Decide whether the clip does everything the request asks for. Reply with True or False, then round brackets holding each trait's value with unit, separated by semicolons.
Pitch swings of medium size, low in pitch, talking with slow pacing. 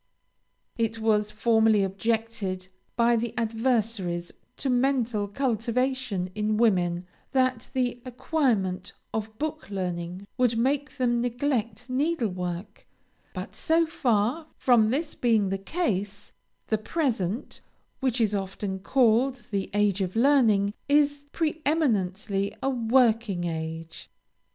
False (4.4 semitones; 225 Hz; 110 wpm)